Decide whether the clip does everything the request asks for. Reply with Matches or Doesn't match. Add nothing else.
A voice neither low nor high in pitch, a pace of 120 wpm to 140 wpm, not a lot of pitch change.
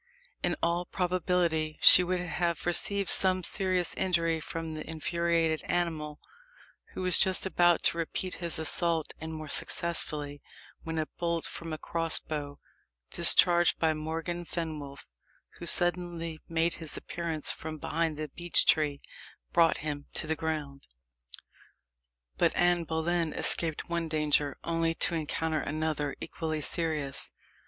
Matches